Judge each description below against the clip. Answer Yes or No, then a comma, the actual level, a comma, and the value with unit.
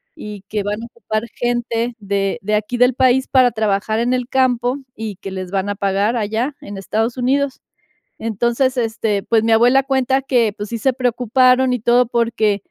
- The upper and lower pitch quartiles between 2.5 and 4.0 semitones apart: Yes, average, 3.0 semitones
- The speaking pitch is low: No, high, 235 Hz